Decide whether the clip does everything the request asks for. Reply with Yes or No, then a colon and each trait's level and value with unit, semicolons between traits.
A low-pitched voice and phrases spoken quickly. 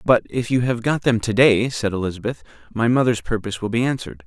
Yes: low, 115 Hz; fast, 225 wpm